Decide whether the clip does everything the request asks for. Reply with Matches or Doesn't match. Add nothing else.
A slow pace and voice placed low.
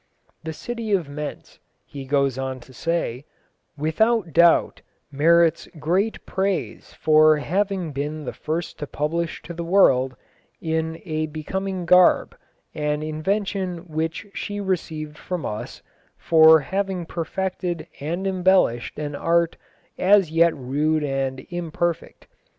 Doesn't match